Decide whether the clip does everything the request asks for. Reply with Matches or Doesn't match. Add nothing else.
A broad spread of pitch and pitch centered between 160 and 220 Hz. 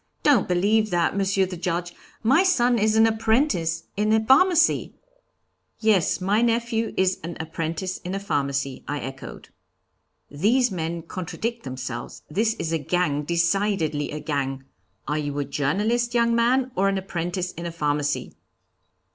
Matches